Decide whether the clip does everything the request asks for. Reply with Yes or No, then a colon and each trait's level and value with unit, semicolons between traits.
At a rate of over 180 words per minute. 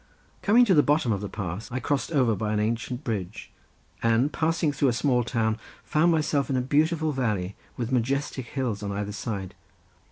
Yes: average, 190 wpm